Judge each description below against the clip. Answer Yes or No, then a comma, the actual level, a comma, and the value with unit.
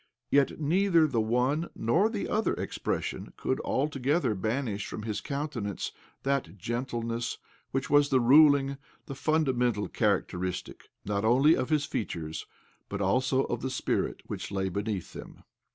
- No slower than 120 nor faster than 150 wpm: Yes, average, 145 wpm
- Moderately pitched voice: No, low, 130 Hz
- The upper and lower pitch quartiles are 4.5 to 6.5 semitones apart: Yes, average, 5.1 semitones